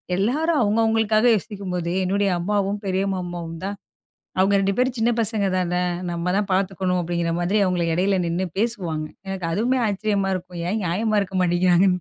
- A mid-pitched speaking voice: No, high, 195 Hz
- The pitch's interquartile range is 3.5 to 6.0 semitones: No, average, 2.9 semitones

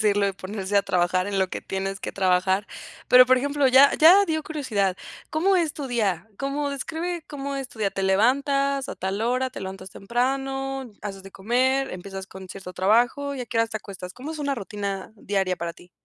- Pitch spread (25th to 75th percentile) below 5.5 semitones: No, wide, 6.1 semitones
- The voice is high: Yes, high, 225 Hz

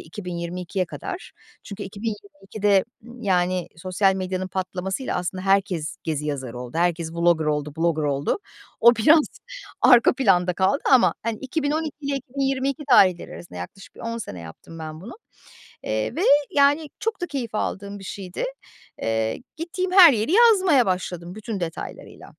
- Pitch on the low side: No, high, 195 Hz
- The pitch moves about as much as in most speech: No, wide, 7.1 semitones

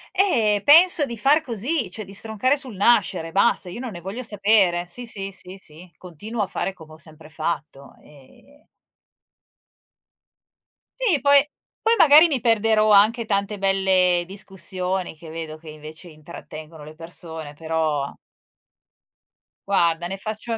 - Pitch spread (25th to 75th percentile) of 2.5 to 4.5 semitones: No, wide, 5.7 semitones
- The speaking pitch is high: Yes, high, 195 Hz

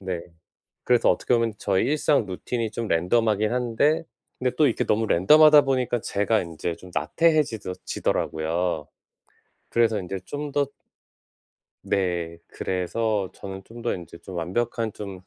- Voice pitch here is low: Yes, low, 110 Hz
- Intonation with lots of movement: No, average, 5.0 semitones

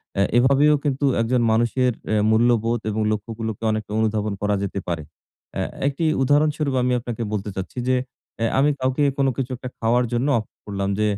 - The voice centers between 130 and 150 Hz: No, low, 120 Hz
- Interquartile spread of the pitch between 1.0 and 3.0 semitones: No, average, 3.4 semitones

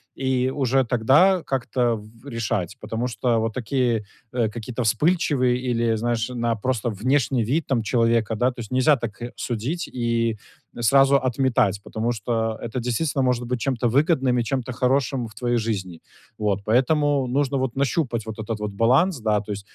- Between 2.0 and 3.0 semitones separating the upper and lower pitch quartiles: Yes, average, 2.7 semitones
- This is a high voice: No, low, 120 Hz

